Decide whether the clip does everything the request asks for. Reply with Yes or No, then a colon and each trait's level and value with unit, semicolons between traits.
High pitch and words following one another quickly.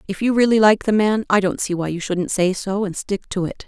Yes: high, 200 Hz; fast, 295 wpm